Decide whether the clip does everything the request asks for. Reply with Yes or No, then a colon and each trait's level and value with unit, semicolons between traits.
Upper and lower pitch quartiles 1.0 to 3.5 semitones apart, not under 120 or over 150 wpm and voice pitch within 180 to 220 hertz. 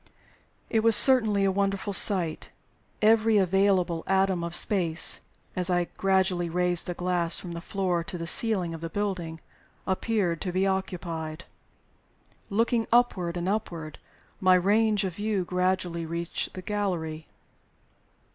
Yes: average, 2.8 semitones; slow, 135 wpm; medium, 185 Hz